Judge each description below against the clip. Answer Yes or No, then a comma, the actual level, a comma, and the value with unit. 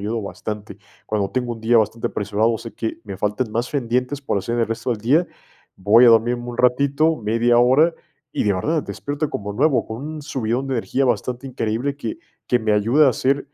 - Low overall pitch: Yes, low, 120 Hz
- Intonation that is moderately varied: Yes, average, 3.6 semitones